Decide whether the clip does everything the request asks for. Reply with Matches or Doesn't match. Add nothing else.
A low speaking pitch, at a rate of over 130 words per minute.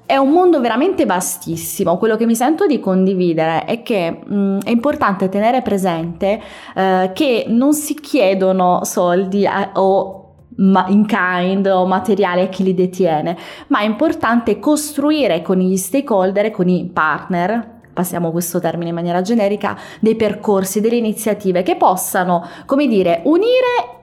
Doesn't match